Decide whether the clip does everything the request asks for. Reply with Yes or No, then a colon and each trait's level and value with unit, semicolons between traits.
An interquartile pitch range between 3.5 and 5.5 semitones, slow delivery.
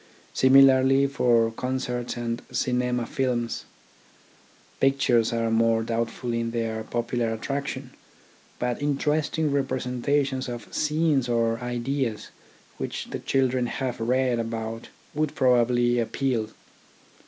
No: narrow, 2.4 semitones; slow, 110 wpm